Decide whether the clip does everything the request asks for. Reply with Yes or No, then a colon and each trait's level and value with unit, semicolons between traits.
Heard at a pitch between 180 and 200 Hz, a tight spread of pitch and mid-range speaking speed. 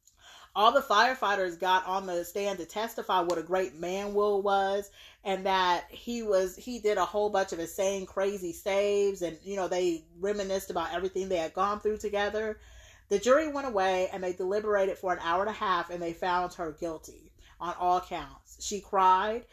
Yes: high, 190 Hz; narrow, 2.3 semitones; average, 195 wpm